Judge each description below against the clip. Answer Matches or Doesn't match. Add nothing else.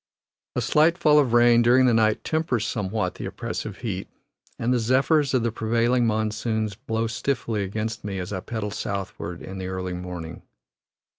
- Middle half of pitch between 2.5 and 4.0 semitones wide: Matches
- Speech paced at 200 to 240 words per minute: Doesn't match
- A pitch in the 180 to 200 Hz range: Doesn't match